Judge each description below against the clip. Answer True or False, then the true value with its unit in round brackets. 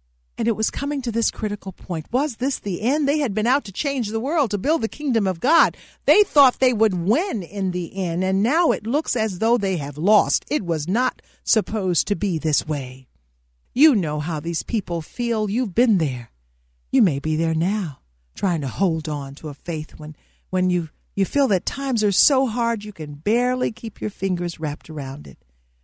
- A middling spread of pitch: False (7.1 semitones)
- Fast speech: True (210 wpm)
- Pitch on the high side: True (195 Hz)